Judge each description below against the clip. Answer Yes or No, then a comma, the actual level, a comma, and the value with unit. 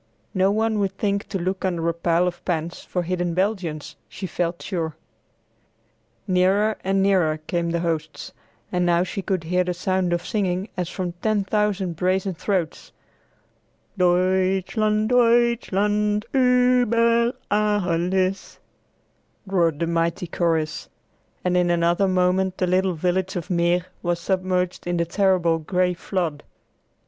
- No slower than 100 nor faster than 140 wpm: Yes, slow, 135 wpm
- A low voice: No, medium, 185 Hz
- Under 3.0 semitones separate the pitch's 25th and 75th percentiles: Yes, narrow, 2.4 semitones